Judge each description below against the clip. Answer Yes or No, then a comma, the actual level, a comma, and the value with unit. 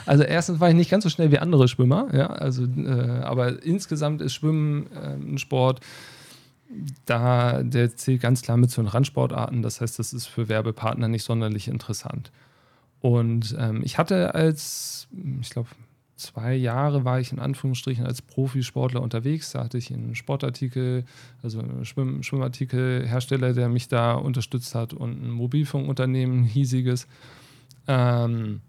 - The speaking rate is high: No, average, 155 wpm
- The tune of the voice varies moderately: No, narrow, 2.3 semitones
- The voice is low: Yes, low, 130 Hz